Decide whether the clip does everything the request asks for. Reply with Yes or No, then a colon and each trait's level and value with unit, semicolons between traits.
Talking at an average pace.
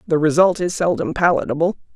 Yes: average, 155 wpm